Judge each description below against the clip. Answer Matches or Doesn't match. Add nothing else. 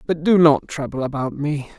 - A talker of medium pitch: Matches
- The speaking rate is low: Doesn't match